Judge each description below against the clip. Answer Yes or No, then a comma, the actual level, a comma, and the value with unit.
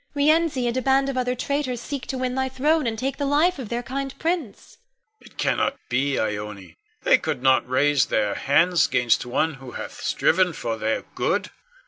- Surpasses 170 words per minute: Yes, average, 195 wpm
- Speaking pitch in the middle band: No, high, 245 Hz